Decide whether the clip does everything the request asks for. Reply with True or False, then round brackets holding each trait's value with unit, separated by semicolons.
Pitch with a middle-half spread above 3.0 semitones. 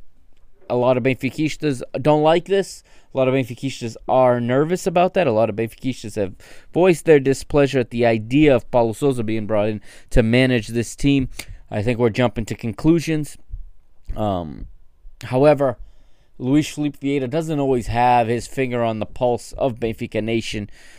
True (4.2 semitones)